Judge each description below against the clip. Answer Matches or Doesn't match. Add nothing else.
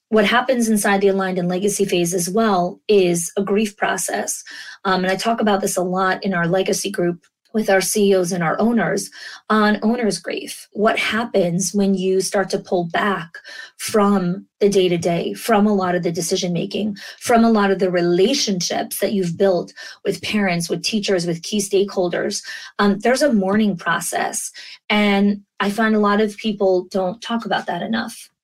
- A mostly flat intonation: Matches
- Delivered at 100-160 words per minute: Doesn't match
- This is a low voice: Doesn't match